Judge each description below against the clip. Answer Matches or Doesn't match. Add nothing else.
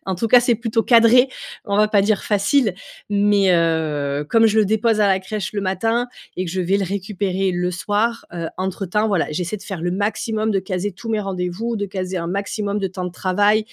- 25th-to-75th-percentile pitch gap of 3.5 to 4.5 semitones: Doesn't match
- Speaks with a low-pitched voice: Doesn't match